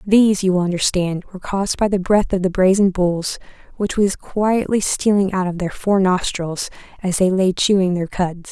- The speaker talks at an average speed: Yes, average, 195 wpm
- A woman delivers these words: Yes, female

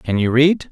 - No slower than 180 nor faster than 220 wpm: No, fast, 250 wpm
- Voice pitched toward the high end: No, low, 135 Hz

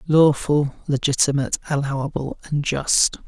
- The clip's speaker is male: Yes, male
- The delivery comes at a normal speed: No, slow, 90 wpm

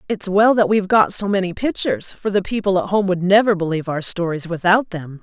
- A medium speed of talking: No, fast, 230 wpm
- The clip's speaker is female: Yes, female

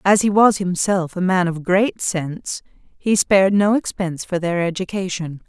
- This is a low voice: No, medium, 185 Hz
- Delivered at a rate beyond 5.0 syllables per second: No, 4.6 syllables/s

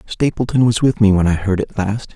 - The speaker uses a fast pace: Yes, fast, 250 wpm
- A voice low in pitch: Yes, low, 110 Hz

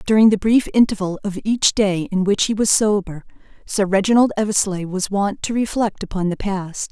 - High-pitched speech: Yes, high, 200 Hz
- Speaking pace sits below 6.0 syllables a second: Yes, 5.1 syllables/s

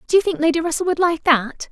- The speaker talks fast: Yes, fast, 280 wpm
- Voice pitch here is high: Yes, very high, 325 Hz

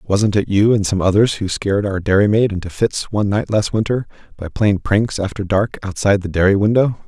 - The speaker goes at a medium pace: No, fast, 210 wpm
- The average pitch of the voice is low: Yes, low, 100 Hz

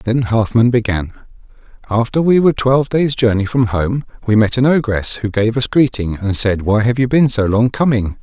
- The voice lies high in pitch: No, low, 115 Hz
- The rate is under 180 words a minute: No, fast, 205 wpm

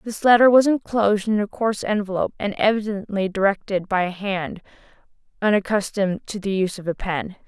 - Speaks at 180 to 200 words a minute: No, average, 170 wpm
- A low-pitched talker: No, high, 195 Hz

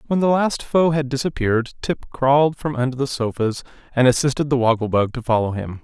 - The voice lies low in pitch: Yes, low, 130 Hz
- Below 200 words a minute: No, fast, 205 wpm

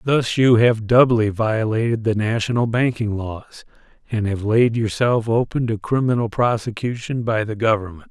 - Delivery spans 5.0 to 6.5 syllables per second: No, 4.7 syllables/s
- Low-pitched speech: Yes, low, 115 Hz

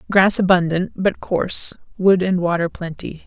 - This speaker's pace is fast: No, average, 145 wpm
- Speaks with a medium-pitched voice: Yes, medium, 180 Hz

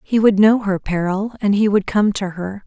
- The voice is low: No, high, 205 Hz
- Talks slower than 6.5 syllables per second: Yes, 4.8 syllables/s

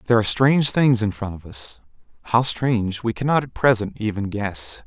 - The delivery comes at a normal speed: Yes, average, 185 wpm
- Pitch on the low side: Yes, low, 110 Hz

